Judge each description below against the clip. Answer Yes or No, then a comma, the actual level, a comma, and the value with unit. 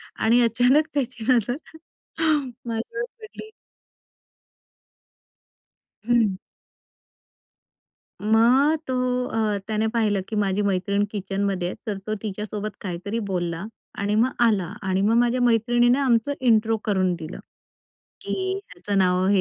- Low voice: No, high, 215 Hz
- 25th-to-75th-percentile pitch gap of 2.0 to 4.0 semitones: Yes, average, 3.5 semitones